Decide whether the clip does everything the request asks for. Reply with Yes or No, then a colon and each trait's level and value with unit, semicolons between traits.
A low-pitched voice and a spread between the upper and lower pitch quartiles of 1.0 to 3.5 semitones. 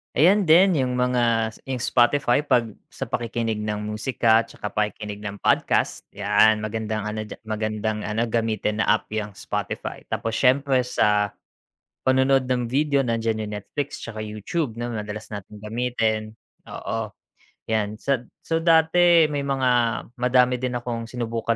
Yes: low, 115 Hz; average, 3.0 semitones